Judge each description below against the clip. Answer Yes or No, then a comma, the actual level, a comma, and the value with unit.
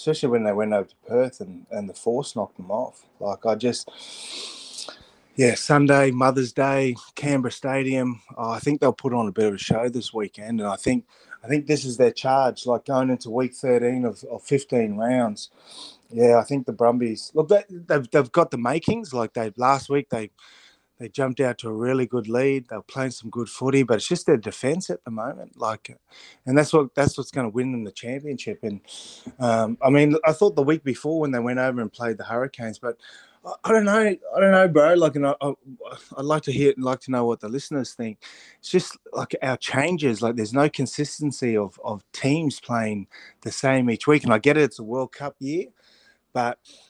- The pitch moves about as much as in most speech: Yes, average, 3.6 semitones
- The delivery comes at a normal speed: No, fast, 220 wpm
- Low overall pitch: Yes, low, 130 Hz